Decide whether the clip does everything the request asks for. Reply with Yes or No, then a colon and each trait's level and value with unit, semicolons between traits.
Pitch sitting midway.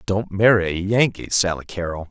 No: low, 100 Hz